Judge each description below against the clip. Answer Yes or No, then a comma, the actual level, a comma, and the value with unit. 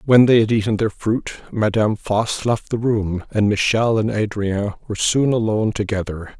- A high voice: No, low, 110 Hz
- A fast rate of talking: No, average, 180 wpm